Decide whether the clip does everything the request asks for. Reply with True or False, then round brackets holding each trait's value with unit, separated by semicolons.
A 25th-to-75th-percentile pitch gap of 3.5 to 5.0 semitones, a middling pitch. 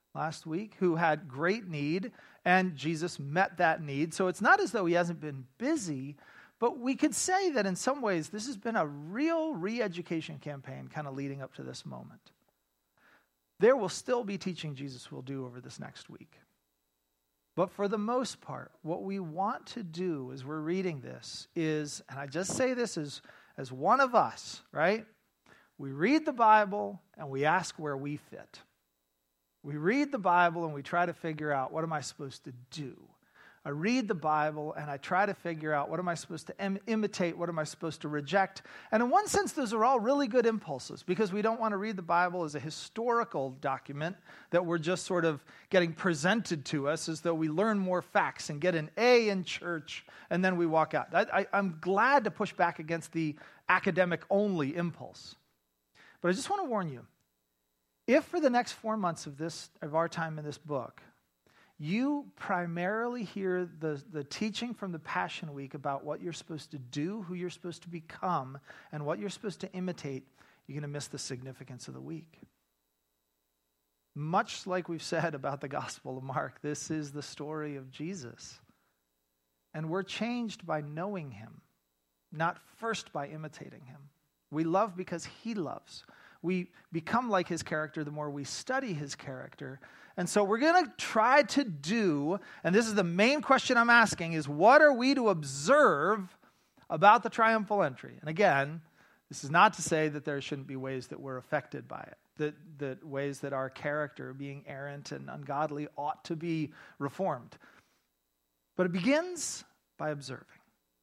False (5.6 semitones; 165 Hz)